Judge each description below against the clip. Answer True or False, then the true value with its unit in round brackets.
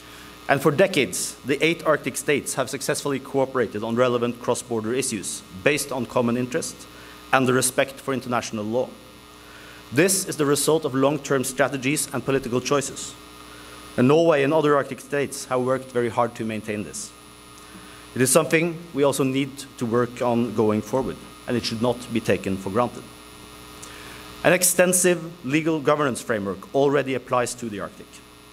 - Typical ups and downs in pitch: True (3.8 semitones)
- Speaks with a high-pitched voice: False (130 Hz)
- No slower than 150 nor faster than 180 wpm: True (160 wpm)